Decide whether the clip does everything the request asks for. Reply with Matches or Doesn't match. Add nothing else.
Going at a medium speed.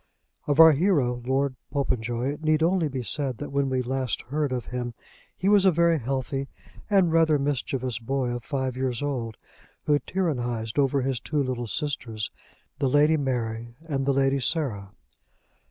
Matches